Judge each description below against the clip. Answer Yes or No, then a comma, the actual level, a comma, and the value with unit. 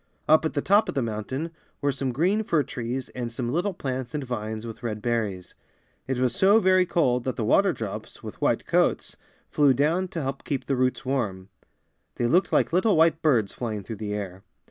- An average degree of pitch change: No, wide, 5.8 semitones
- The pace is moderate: No, fast, 210 wpm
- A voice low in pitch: Yes, low, 130 Hz